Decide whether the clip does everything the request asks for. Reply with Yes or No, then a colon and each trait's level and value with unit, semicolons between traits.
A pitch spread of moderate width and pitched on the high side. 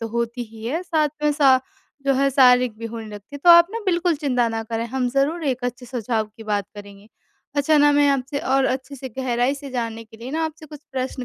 Yes: average, 3.8 semitones; very high, 260 Hz